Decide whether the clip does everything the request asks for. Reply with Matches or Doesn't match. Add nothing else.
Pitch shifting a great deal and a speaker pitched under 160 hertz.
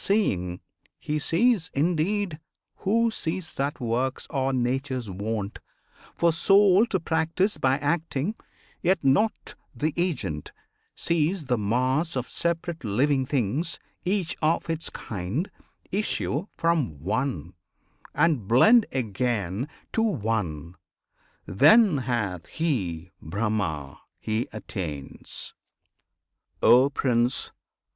Matches